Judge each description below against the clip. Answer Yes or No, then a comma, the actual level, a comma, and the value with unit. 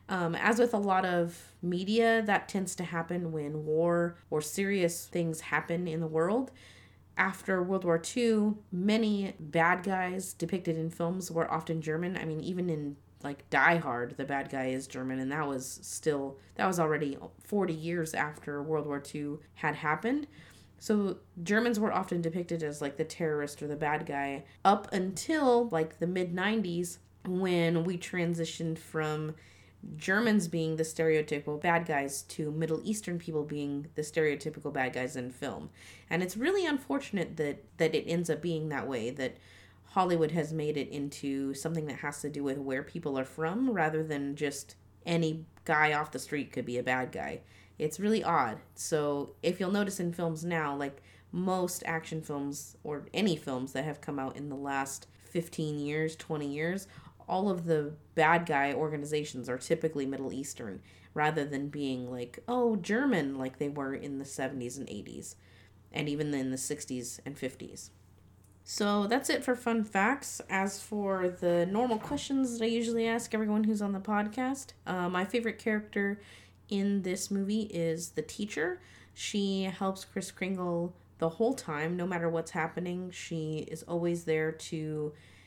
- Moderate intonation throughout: Yes, average, 4.6 semitones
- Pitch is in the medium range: Yes, medium, 160 Hz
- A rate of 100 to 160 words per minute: No, average, 175 wpm